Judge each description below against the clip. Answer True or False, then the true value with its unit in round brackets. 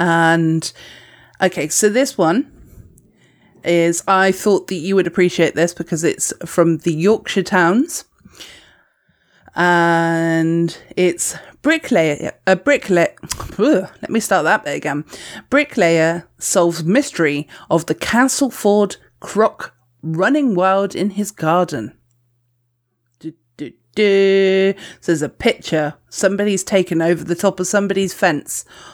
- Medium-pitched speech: True (175 Hz)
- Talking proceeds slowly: True (120 wpm)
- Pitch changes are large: False (3.6 semitones)